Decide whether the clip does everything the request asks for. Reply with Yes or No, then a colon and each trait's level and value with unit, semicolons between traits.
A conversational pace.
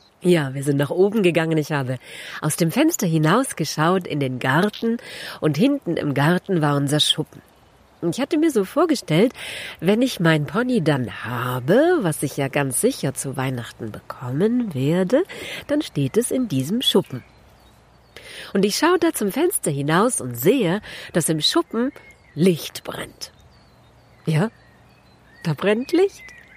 Yes: average, 150 wpm